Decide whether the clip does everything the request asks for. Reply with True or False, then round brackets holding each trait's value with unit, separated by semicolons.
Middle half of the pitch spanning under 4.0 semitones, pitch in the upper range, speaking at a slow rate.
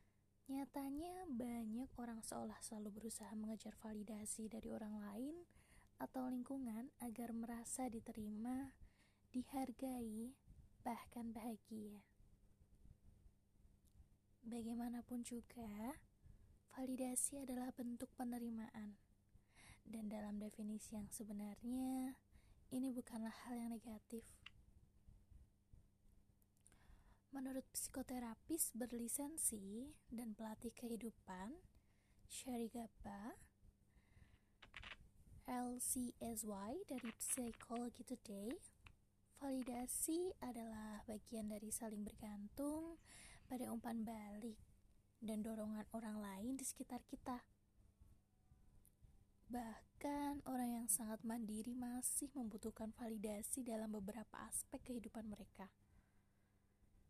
True (3.0 semitones; 230 Hz; 80 wpm)